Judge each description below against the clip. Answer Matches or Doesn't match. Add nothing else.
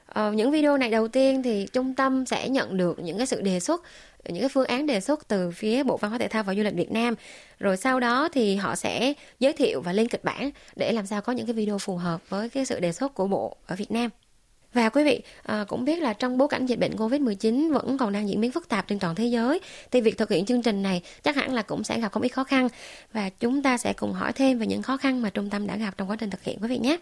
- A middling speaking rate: Doesn't match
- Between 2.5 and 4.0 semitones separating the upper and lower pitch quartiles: Doesn't match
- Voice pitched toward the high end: Matches